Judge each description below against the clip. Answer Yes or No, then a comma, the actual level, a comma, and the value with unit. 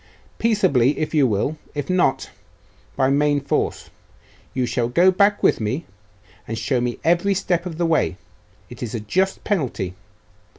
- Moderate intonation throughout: No, wide, 6.5 semitones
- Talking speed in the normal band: Yes, average, 160 wpm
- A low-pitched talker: No, medium, 145 Hz